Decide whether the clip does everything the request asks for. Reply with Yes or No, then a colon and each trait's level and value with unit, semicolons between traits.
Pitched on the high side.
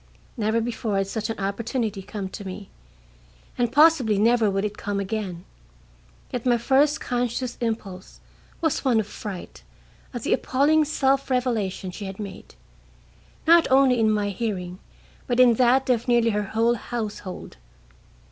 Yes: high, 225 Hz